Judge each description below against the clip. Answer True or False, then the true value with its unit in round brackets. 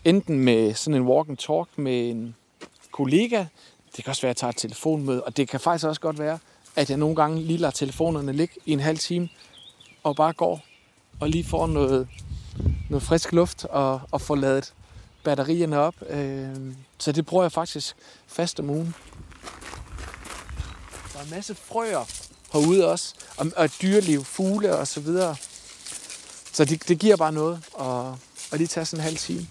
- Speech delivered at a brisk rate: False (185 wpm)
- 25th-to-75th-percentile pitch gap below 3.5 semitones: False (4.0 semitones)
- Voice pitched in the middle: True (150 Hz)